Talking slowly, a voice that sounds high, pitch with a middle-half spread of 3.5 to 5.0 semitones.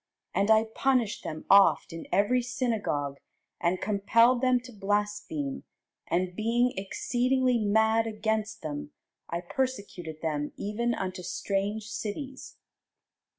Yes: slow, 115 wpm; high, 210 Hz; average, 4.4 semitones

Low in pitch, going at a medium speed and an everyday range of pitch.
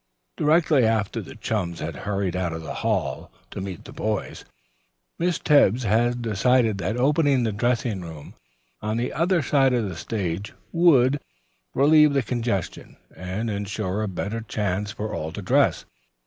Yes: low, 110 Hz; average, 160 wpm; average, 4.7 semitones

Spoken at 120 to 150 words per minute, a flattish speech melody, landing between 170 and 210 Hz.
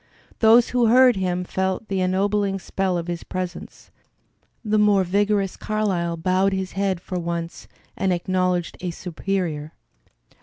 Yes: average, 140 wpm; narrow, 2.2 semitones; high, 190 Hz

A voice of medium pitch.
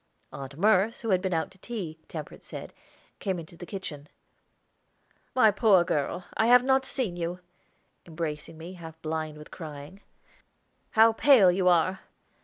Yes: medium, 180 Hz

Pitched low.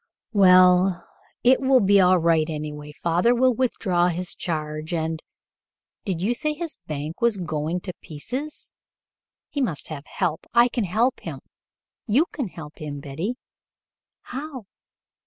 No: medium, 180 Hz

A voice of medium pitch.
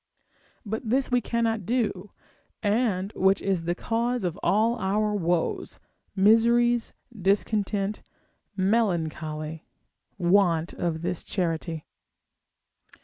No: high, 200 Hz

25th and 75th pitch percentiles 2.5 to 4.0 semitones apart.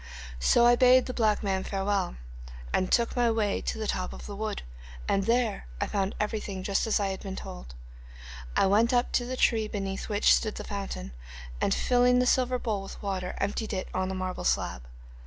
Yes: average, 3.4 semitones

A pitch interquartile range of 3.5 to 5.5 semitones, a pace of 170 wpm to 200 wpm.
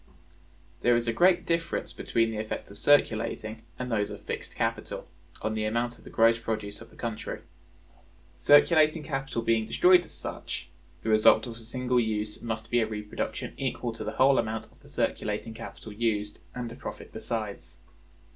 No: narrow, 2.5 semitones; average, 180 wpm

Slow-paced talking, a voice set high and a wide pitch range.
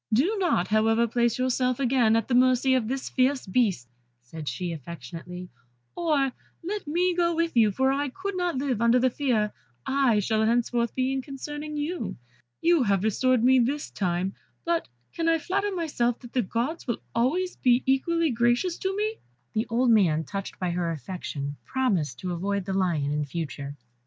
No: average, 185 wpm; high, 245 Hz; wide, 6.7 semitones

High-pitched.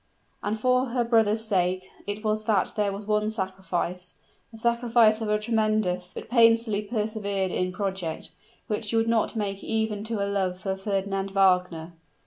Yes: high, 210 Hz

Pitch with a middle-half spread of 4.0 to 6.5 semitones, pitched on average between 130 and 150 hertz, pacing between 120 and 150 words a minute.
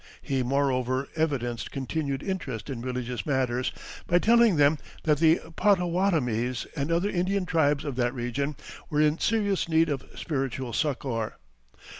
Yes: average, 4.6 semitones; medium, 140 Hz; average, 140 wpm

